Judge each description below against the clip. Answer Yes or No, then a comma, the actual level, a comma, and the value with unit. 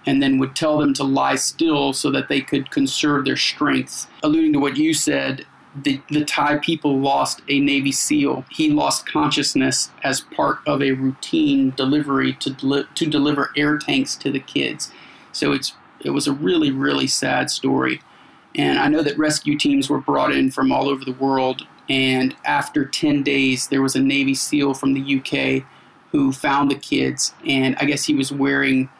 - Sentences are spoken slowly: No, average, 190 wpm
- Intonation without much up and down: Yes, narrow, 2.0 semitones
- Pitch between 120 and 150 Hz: Yes, medium, 140 Hz